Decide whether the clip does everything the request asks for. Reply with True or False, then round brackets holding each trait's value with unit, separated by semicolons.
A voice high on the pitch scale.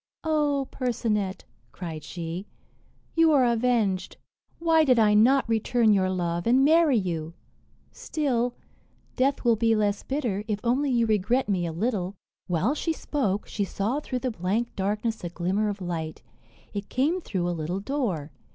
True (220 Hz)